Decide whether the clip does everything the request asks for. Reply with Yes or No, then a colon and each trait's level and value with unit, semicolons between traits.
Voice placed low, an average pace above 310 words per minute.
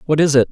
No: medium, 145 Hz; fast, 350 wpm